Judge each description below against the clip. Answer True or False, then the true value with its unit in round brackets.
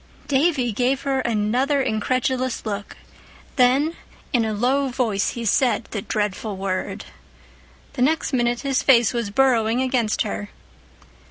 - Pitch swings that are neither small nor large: True (3.6 semitones)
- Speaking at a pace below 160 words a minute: True (140 wpm)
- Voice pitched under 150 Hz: False (245 Hz)